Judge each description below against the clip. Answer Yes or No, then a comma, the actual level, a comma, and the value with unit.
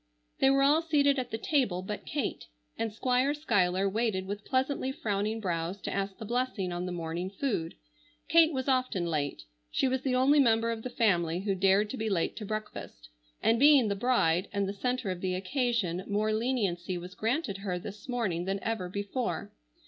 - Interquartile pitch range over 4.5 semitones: Yes, wide, 5.4 semitones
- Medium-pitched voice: No, high, 215 Hz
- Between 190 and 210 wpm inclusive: Yes, average, 195 wpm